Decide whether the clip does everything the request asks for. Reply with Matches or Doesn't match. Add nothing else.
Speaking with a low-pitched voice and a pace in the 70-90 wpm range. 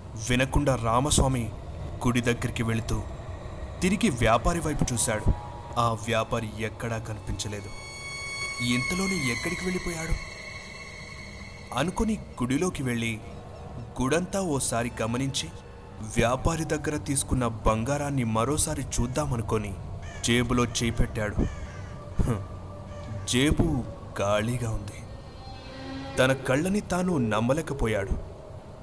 Matches